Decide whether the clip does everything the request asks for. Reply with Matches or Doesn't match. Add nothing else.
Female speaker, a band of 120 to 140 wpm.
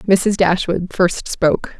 Matches